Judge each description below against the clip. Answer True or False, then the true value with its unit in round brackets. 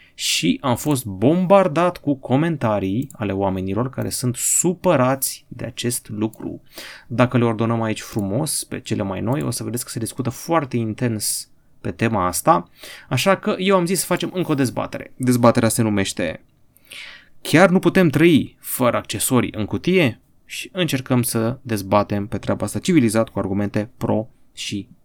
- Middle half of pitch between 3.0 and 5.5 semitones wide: True (5.2 semitones)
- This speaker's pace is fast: False (160 wpm)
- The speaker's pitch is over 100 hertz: True (120 Hz)